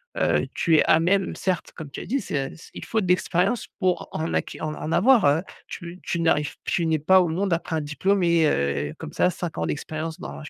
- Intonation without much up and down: No, average, 3.3 semitones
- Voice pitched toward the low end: No, medium, 165 Hz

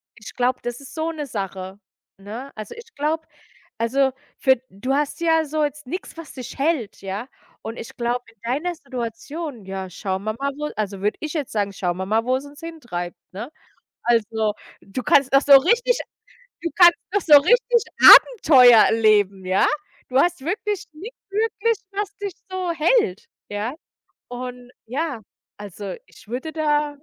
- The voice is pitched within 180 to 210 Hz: No, very high, 265 Hz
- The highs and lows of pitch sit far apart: Yes, wide, 6.9 semitones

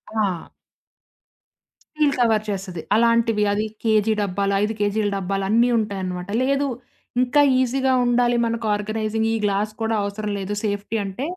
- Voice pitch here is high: Yes, high, 215 Hz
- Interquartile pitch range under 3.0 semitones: Yes, narrow, 2.5 semitones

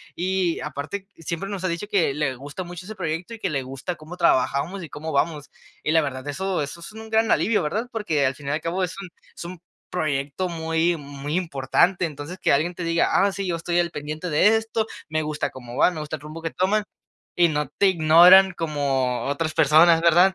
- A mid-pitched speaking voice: Yes, medium, 165 Hz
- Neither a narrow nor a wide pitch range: Yes, average, 3.7 semitones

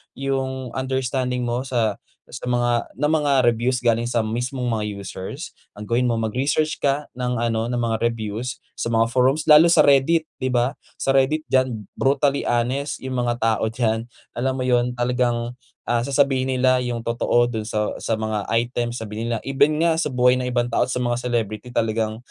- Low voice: Yes, low, 125 Hz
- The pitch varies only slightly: Yes, narrow, 2.2 semitones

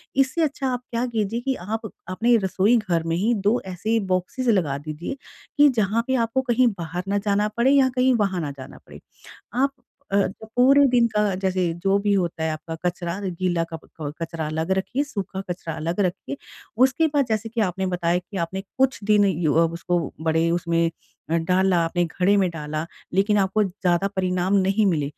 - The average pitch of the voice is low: No, high, 190 Hz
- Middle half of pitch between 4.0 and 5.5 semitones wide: Yes, average, 5.0 semitones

